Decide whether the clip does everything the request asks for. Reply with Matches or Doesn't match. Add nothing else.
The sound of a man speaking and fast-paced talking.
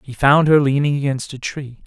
Matches